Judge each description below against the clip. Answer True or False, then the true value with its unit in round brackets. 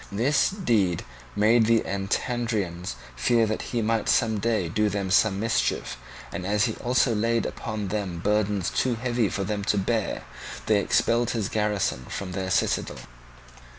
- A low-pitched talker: True (105 Hz)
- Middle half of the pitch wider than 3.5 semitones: False (2.9 semitones)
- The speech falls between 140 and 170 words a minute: True (155 wpm)